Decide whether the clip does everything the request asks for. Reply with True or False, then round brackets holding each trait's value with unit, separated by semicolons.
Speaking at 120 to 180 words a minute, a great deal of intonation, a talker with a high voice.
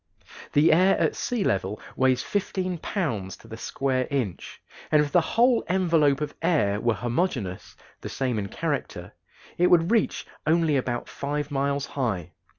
False (155 wpm; 6.0 semitones; 140 Hz)